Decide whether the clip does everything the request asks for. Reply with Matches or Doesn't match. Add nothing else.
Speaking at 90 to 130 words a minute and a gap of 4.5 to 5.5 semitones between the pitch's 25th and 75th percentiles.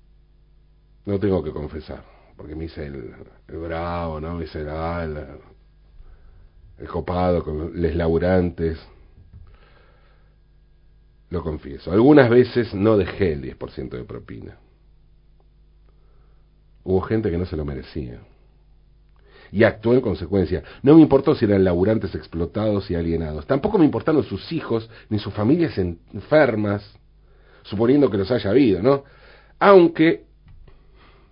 Matches